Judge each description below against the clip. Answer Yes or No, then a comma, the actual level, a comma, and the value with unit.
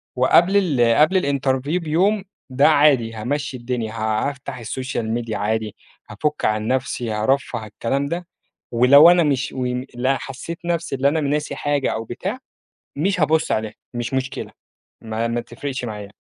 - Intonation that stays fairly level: No, average, 4.4 semitones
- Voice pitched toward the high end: No, low, 130 Hz